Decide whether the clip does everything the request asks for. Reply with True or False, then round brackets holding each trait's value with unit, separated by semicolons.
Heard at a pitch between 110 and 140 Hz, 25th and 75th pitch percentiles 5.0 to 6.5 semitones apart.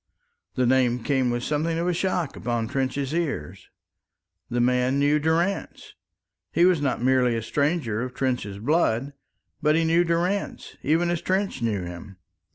True (135 Hz; 5.4 semitones)